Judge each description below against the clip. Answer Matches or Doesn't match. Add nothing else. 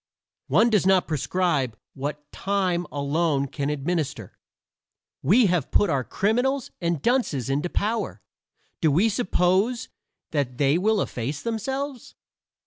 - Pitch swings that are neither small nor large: Doesn't match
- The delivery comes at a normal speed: Doesn't match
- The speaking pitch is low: Doesn't match